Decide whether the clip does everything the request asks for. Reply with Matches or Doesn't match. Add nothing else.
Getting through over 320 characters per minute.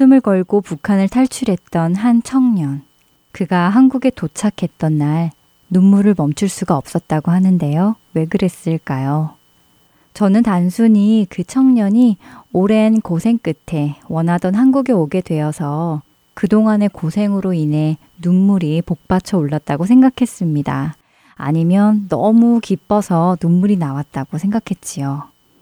Doesn't match